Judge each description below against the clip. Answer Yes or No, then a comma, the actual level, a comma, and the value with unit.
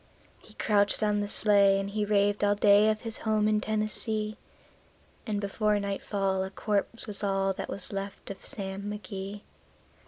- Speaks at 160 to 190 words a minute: Yes, average, 165 wpm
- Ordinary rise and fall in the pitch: No, narrow, 1.3 semitones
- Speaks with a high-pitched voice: Yes, high, 205 Hz